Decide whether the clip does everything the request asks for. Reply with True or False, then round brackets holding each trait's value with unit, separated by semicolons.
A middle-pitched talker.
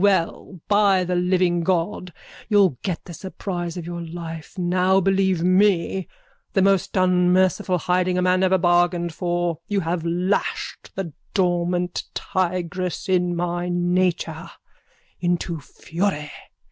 True (180 Hz)